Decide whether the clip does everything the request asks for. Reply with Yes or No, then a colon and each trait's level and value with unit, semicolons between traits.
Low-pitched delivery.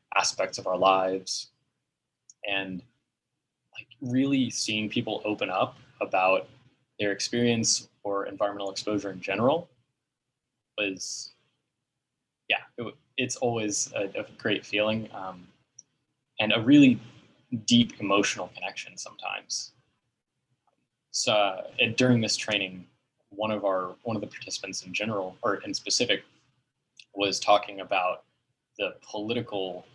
Yes: low, 105 Hz